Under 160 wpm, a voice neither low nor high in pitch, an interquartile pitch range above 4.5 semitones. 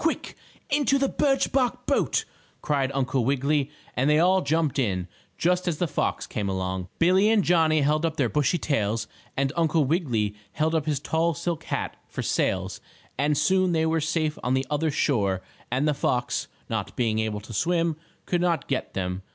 No: average, 185 wpm; medium, 150 Hz; average, 5.0 semitones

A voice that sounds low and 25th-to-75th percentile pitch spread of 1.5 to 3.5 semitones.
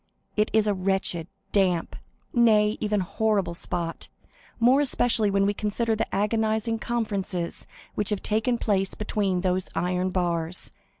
No: high, 205 Hz; average, 3.2 semitones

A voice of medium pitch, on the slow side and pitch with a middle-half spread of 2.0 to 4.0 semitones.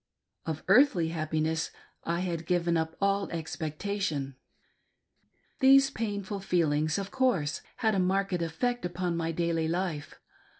Yes: medium, 175 Hz; slow, 125 wpm; average, 3.6 semitones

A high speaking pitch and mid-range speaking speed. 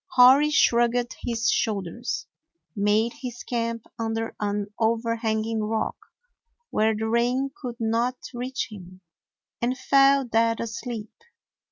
No: high, 230 Hz; slow, 115 wpm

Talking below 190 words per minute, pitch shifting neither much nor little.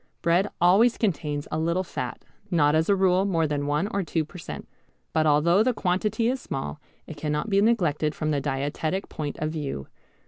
No: average, 195 wpm; average, 4.5 semitones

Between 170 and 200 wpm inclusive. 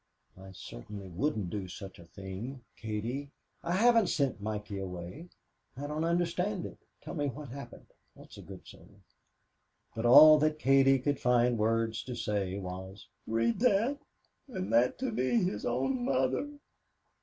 No: average, 155 wpm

